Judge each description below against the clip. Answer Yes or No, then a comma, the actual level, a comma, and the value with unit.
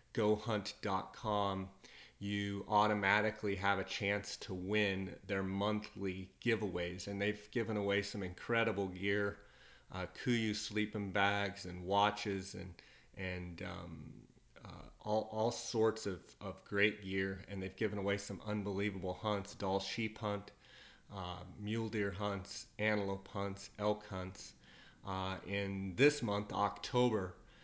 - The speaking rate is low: Yes, slow, 125 wpm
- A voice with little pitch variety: Yes, narrow, 1.6 semitones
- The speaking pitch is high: No, low, 100 Hz